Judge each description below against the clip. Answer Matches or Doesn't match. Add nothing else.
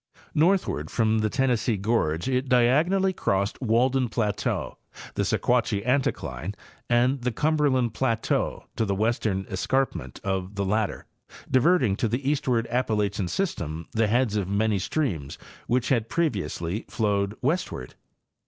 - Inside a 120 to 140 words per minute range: Matches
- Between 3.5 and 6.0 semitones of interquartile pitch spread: Matches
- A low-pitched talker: Matches